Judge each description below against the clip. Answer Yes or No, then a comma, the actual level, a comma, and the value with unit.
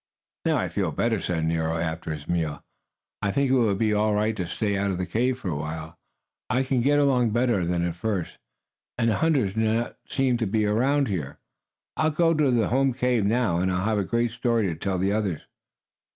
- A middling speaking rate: No, fast, 225 wpm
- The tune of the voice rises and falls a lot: Yes, wide, 5.7 semitones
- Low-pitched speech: Yes, low, 110 Hz